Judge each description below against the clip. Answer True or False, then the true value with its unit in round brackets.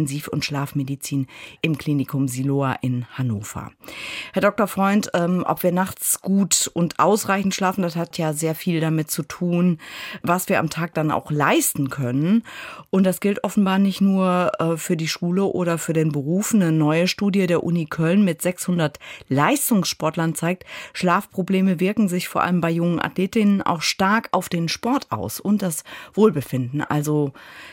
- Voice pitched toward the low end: False (170 Hz)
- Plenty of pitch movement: False (4.0 semitones)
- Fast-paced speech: False (160 wpm)